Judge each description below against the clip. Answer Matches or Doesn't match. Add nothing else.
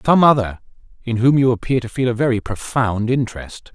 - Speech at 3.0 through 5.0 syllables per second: Doesn't match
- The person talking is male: Matches